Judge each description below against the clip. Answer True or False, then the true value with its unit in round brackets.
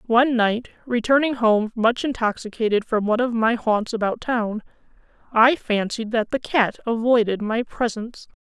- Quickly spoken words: False (150 wpm)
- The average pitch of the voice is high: True (230 Hz)